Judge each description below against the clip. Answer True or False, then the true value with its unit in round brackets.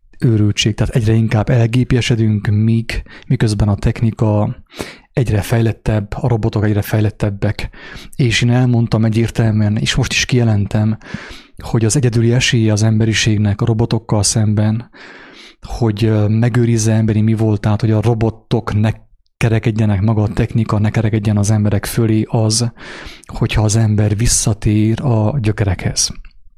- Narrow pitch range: True (1.6 semitones)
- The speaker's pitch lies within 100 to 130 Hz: True (110 Hz)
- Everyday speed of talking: False (125 wpm)